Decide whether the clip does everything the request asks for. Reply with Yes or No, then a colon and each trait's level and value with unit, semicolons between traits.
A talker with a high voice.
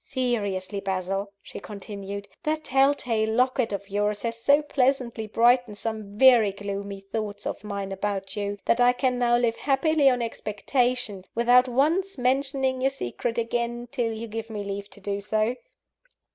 Yes: high, 230 Hz